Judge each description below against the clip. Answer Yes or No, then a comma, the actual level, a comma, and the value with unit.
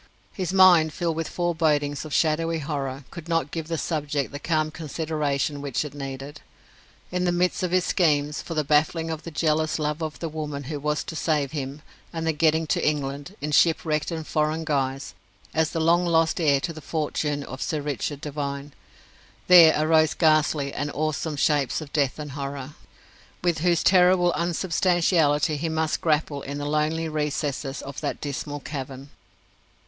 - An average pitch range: No, narrow, 2.1 semitones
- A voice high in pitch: No, medium, 155 Hz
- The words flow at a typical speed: Yes, average, 175 wpm